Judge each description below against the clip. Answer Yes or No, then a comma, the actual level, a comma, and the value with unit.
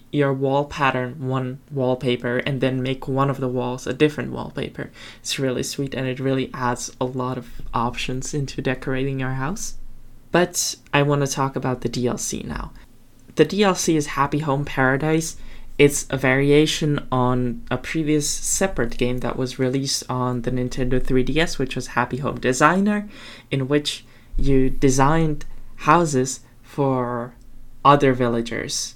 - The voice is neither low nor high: No, low, 130 Hz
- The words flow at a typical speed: Yes, average, 150 wpm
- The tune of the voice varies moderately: No, narrow, 2.2 semitones